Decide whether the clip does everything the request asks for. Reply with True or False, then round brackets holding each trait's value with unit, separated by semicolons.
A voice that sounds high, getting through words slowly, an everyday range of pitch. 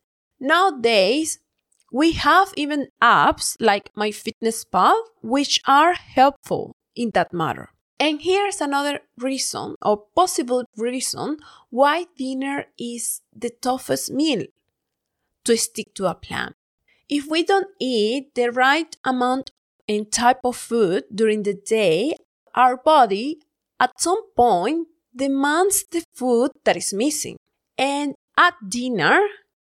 True (265 Hz; 120 wpm; 5.0 semitones)